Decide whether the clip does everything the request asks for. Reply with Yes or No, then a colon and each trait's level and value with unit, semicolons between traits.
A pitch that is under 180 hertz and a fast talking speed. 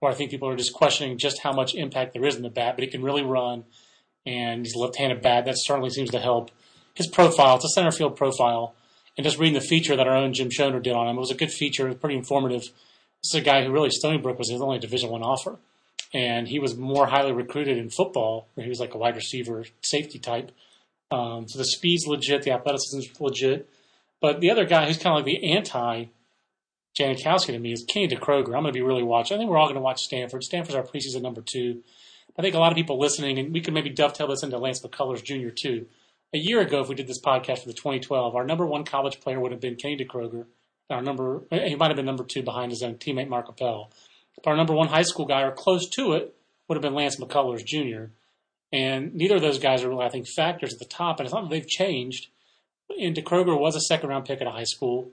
Yes: low, 135 Hz; fast, 255 wpm